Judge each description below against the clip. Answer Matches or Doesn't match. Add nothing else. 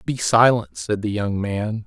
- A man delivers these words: Matches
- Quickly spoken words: Doesn't match